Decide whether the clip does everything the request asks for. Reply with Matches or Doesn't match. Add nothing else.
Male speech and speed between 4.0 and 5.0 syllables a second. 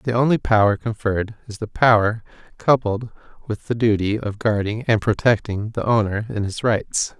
Matches